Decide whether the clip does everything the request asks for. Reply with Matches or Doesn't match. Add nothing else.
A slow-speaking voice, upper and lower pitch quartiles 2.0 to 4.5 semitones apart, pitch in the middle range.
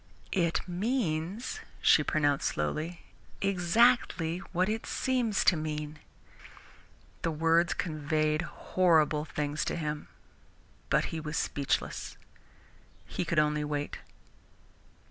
Matches